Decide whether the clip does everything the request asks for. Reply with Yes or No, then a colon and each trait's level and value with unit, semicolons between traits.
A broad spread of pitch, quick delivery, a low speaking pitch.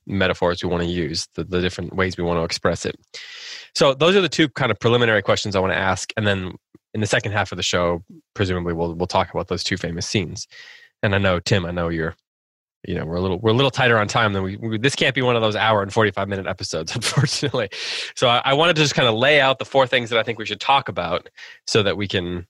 Yes: wide, 5.8 semitones; fast, 270 wpm; low, 100 Hz